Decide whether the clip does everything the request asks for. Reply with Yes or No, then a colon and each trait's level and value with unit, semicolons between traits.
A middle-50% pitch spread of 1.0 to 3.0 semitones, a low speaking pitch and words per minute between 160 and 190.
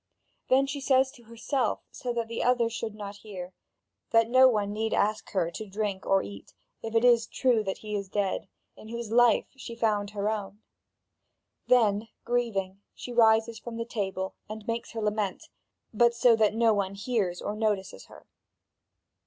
No: narrow, 2.5 semitones; high, 220 Hz; average, 180 wpm